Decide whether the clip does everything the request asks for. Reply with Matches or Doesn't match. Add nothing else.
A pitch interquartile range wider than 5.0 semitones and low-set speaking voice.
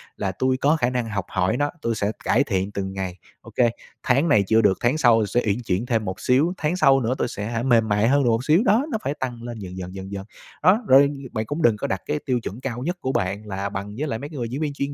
Matches